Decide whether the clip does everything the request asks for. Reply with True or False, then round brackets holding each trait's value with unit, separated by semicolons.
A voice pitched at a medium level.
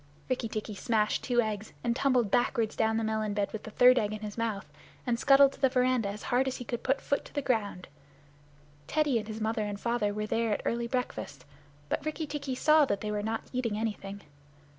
False (225 Hz)